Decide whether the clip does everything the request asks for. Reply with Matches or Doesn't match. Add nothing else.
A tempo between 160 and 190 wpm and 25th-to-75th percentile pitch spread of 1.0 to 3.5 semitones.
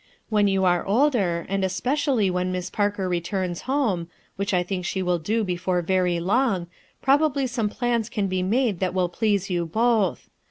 Doesn't match